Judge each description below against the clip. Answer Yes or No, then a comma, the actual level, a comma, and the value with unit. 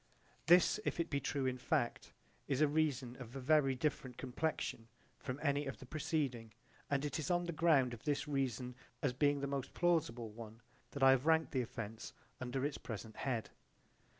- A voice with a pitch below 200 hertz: Yes, low, 135 Hz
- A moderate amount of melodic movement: Yes, average, 3.4 semitones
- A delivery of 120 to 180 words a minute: No, average, 195 wpm